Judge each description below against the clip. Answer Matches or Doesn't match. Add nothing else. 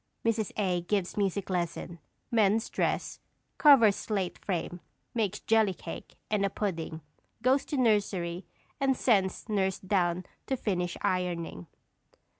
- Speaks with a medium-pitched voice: Doesn't match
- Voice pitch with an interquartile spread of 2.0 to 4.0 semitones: Matches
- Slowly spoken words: Matches